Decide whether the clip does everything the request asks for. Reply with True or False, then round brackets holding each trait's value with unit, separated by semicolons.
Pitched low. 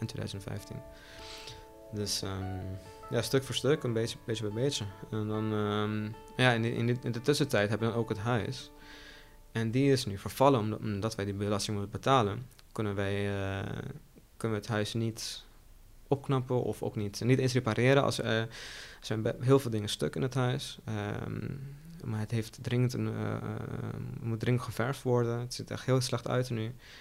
True (115 Hz)